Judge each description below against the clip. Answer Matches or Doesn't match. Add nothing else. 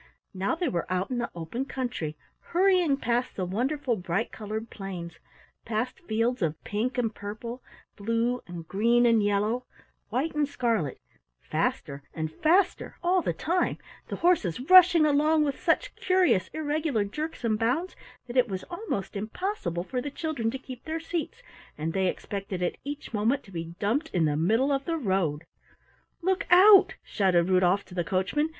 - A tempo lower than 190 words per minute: Matches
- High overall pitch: Matches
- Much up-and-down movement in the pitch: Matches